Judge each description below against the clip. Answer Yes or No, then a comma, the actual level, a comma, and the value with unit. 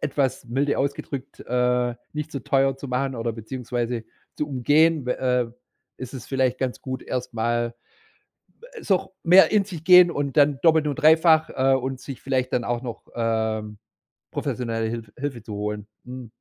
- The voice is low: Yes, low, 130 Hz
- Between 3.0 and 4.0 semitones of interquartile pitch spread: Yes, average, 3.4 semitones